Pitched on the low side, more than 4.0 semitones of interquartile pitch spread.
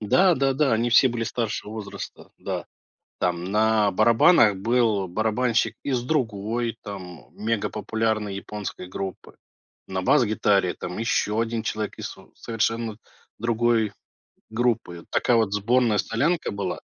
No: low, 110 Hz; narrow, 2.5 semitones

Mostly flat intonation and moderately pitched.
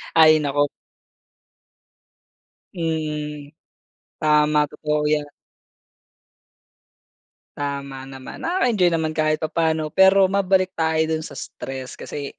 Yes: narrow, 2.0 semitones; medium, 155 Hz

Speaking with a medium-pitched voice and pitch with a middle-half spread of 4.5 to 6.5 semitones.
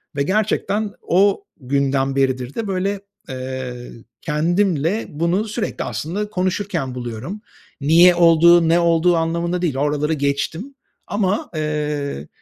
Yes: medium, 165 Hz; average, 5.1 semitones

